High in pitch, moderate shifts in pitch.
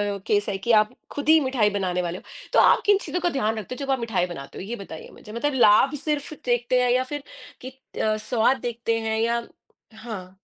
Yes: high, 230 Hz; average, 4.0 semitones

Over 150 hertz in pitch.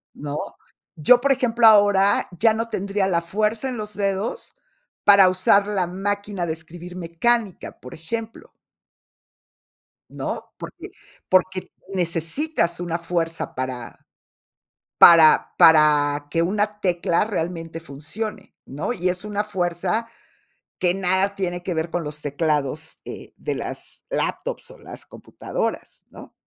Yes: medium, 185 Hz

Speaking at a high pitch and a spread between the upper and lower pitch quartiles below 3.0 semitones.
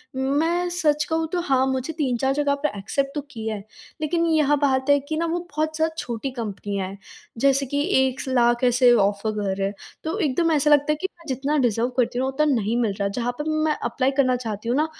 No: very high, 265 Hz; average, 4.3 semitones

